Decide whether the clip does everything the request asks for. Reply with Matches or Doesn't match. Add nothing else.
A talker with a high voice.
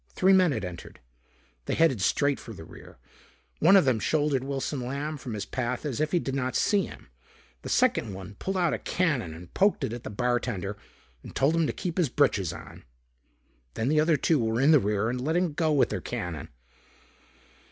Doesn't match